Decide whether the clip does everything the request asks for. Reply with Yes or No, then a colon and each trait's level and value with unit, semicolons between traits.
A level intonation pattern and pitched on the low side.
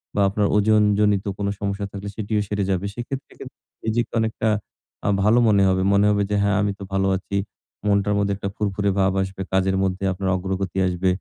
Yes: narrow, 1.3 semitones; low, 100 Hz